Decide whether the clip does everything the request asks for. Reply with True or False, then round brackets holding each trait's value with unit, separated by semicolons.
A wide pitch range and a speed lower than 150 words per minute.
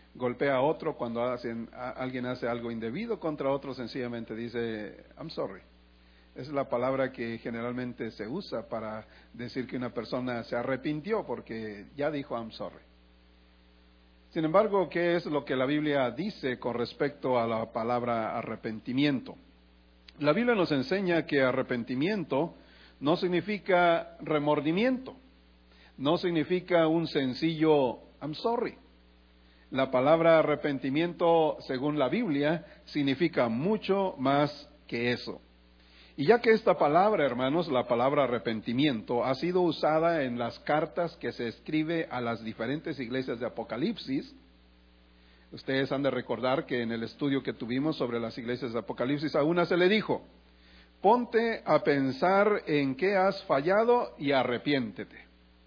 True (5.7 semitones; 140 wpm)